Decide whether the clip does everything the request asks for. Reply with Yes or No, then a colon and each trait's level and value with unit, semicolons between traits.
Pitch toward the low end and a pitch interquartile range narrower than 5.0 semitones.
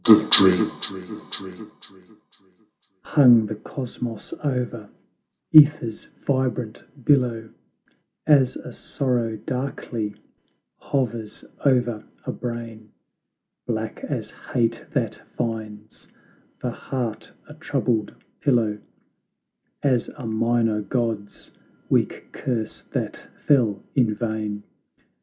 Yes: low, 115 Hz; average, 2.9 semitones